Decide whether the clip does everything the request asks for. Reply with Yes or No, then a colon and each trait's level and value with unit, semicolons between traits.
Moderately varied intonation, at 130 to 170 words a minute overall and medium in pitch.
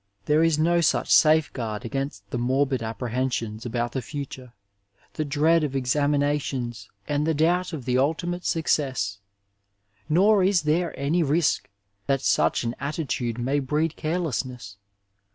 Yes: average, 4.2 semitones; average, 145 wpm; medium, 145 Hz